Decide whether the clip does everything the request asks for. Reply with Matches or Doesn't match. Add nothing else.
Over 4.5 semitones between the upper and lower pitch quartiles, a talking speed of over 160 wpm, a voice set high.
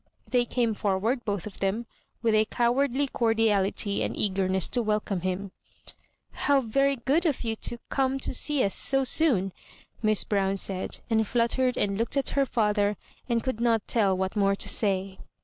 Doesn't match